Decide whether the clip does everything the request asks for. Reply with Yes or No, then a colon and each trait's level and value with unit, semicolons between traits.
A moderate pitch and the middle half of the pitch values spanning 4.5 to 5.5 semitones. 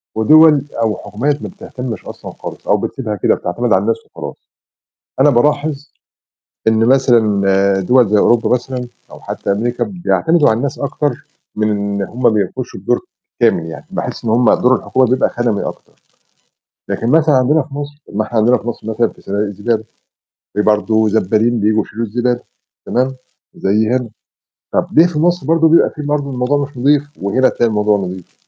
No: low, 120 Hz; average, 4.9 semitones